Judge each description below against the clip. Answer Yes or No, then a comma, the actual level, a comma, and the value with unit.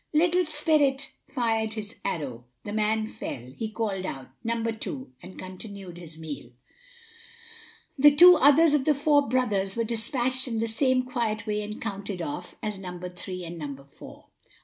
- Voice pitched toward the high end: Yes, high, 220 Hz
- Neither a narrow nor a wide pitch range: No, wide, 6.0 semitones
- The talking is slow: No, average, 165 wpm